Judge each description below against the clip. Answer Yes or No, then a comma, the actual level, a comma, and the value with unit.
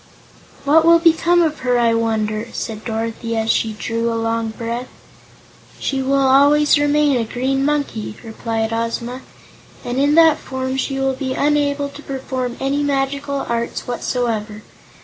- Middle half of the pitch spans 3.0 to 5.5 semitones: Yes, average, 3.7 semitones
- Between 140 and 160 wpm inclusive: Yes, average, 150 wpm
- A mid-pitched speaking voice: No, very high, 260 Hz